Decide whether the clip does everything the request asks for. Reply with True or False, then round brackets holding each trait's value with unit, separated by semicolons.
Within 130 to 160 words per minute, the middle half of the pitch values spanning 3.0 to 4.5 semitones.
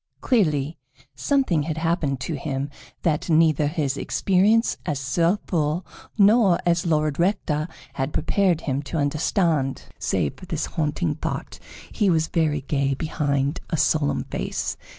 True (140 wpm; 3.3 semitones)